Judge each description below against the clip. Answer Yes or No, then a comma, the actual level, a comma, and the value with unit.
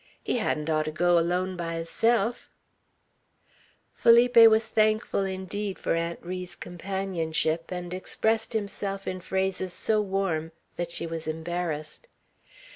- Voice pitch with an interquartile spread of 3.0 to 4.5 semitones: Yes, average, 3.6 semitones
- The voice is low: No, medium, 185 Hz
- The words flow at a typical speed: No, slow, 120 wpm